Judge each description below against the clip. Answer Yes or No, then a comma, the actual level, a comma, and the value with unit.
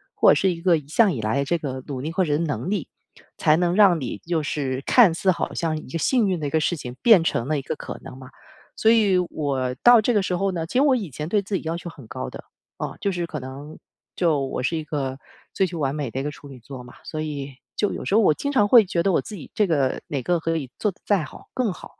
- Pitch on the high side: No, medium, 165 Hz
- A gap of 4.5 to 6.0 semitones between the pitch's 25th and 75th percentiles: Yes, wide, 5.4 semitones